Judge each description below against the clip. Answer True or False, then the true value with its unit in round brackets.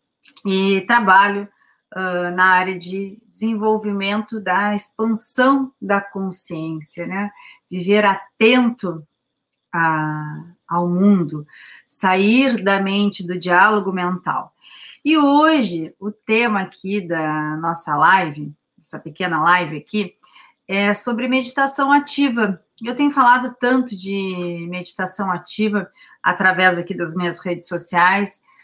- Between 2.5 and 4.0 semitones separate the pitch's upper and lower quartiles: True (3.5 semitones)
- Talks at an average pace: False (110 wpm)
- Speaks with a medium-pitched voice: False (195 Hz)